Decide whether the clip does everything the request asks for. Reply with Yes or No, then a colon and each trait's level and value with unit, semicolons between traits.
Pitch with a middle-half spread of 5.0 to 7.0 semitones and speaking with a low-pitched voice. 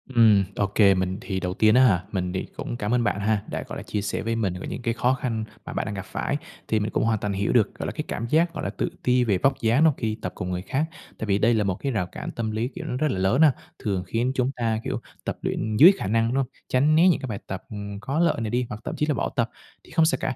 No: average, 4.2 semitones; low, 110 Hz